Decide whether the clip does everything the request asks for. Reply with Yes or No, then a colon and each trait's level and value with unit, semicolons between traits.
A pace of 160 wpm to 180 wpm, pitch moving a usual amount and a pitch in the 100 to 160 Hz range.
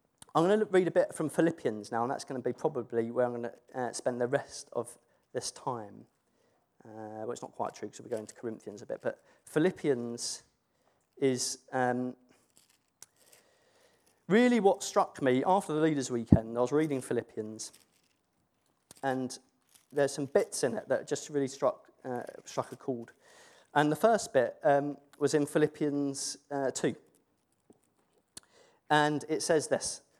Yes: average, 165 wpm; average, 4.8 semitones; medium, 140 Hz